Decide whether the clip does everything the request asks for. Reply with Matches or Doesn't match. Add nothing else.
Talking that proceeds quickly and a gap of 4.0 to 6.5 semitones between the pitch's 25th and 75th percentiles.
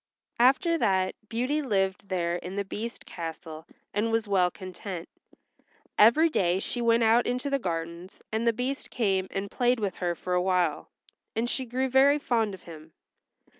Doesn't match